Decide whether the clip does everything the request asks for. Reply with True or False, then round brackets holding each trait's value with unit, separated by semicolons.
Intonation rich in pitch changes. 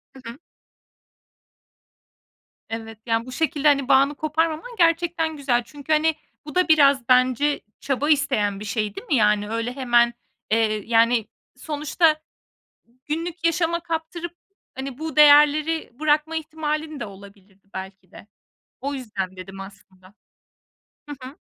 True (5.8 semitones)